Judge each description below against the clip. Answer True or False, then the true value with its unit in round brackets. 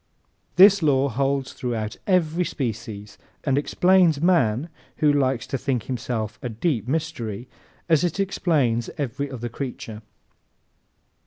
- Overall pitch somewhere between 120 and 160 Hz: True (135 Hz)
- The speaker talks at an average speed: False (125 wpm)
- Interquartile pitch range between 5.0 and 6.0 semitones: True (5.4 semitones)